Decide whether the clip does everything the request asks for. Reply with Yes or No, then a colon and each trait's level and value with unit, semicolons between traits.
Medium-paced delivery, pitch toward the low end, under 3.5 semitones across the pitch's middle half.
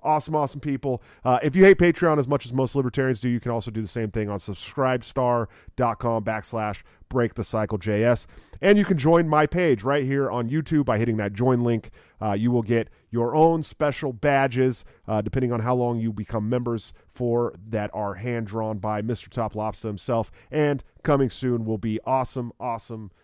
No: average, 185 wpm; low, 120 Hz; average, 3.8 semitones